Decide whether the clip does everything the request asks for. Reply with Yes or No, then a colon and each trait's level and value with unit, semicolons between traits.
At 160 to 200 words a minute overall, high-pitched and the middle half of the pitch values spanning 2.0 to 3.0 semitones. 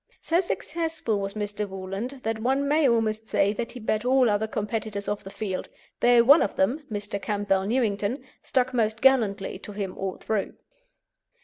No: average, 175 wpm; high, 220 Hz; average, 3.8 semitones